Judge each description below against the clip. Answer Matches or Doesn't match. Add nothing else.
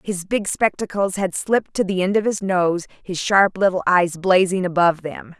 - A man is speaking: Doesn't match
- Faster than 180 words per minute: Matches